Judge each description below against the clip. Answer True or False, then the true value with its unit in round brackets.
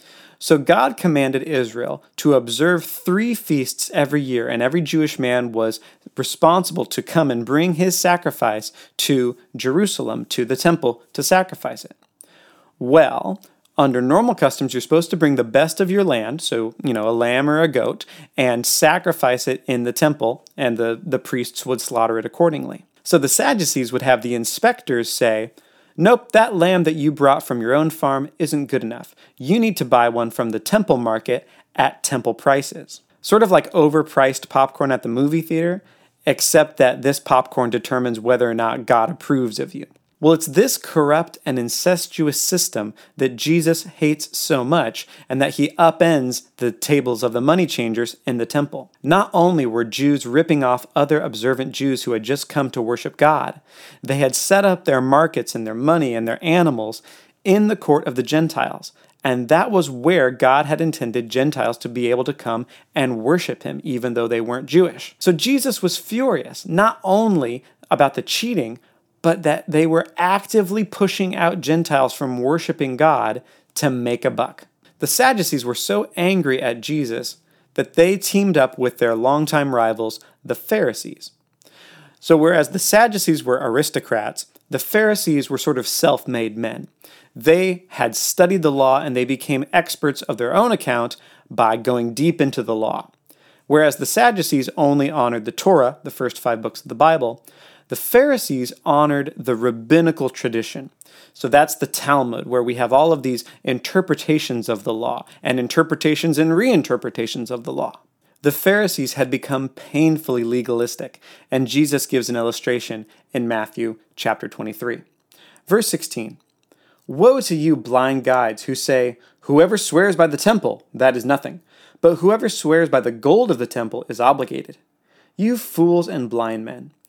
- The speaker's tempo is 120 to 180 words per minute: True (170 wpm)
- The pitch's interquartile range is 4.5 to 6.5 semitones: True (5.1 semitones)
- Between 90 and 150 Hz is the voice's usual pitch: True (140 Hz)